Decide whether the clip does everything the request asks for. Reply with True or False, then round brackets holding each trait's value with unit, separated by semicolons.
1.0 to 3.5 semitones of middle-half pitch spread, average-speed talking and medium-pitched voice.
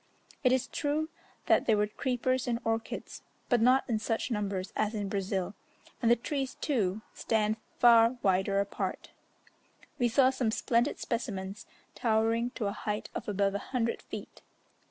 False (3.2 semitones; 155 wpm; 225 Hz)